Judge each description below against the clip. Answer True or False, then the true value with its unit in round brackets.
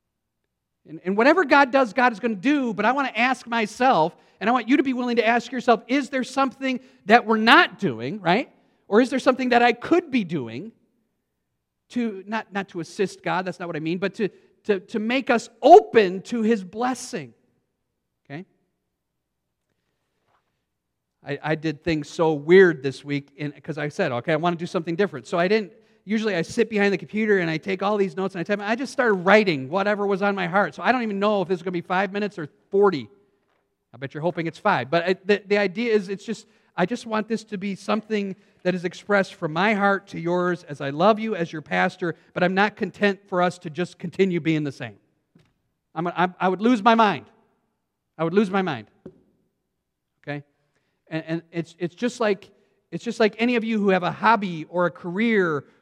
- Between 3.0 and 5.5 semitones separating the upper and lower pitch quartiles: True (5.0 semitones)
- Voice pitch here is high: True (200 Hz)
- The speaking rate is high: True (220 wpm)